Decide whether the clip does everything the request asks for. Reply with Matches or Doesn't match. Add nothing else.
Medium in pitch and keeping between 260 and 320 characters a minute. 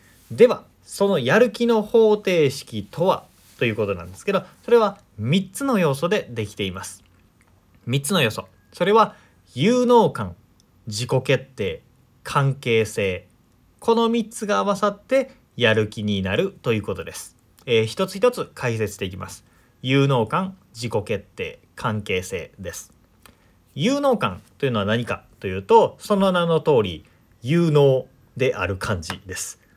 Doesn't match